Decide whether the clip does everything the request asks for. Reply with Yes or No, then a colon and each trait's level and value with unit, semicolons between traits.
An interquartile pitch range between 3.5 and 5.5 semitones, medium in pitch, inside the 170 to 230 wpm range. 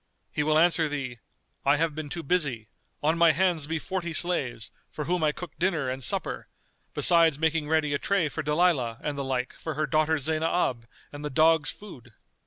No: average, 2.8 semitones; medium, 155 Hz; average, 190 wpm